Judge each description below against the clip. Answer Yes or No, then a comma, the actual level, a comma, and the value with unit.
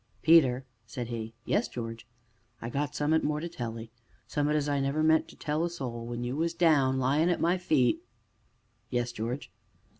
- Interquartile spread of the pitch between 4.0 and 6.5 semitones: Yes, average, 4.5 semitones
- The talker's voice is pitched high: No, medium, 140 Hz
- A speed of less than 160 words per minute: No, average, 200 wpm